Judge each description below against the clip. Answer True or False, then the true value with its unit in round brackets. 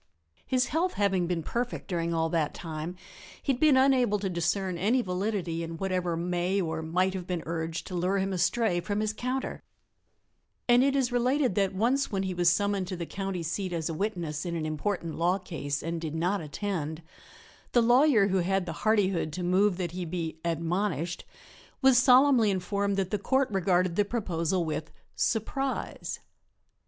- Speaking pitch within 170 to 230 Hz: True (185 Hz)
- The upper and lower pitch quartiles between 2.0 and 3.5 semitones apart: False (3.9 semitones)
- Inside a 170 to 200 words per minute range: True (180 wpm)